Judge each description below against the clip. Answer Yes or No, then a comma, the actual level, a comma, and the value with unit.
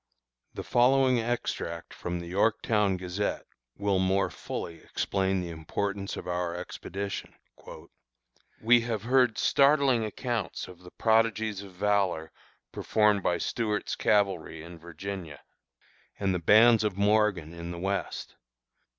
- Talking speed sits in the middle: No, slow, 125 wpm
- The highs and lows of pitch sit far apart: No, average, 3.8 semitones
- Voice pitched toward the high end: No, low, 100 Hz